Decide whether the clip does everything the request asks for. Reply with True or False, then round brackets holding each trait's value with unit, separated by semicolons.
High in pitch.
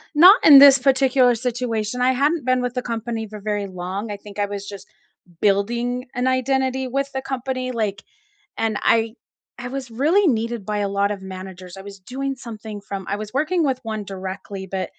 True (230 Hz)